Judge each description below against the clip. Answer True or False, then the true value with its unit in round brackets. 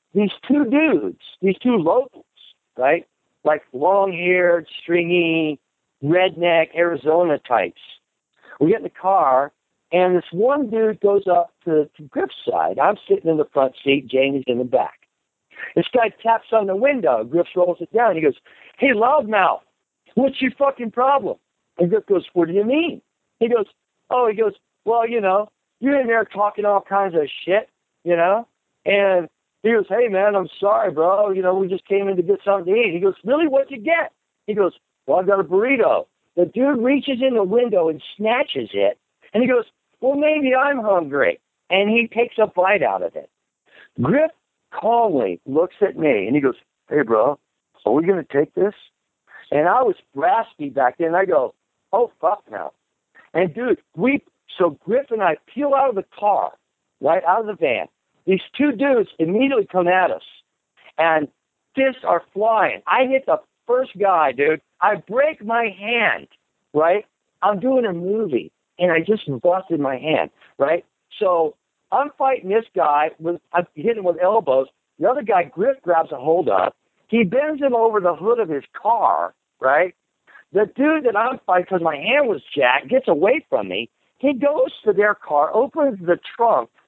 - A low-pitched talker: False (210 Hz)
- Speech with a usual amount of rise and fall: False (7.2 semitones)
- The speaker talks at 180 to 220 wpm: True (185 wpm)